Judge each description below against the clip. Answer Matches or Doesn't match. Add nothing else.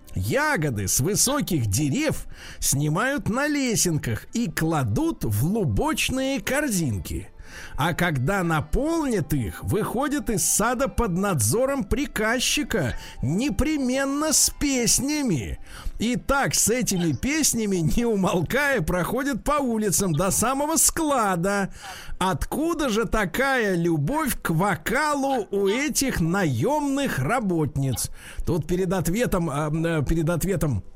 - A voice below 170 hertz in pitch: Doesn't match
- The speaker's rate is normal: Doesn't match